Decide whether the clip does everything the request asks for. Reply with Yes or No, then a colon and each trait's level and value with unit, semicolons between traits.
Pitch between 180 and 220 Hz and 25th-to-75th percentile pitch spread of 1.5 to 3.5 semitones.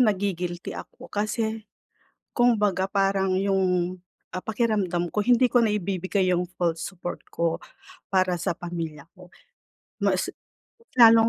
Yes: high, 190 Hz; average, 3.0 semitones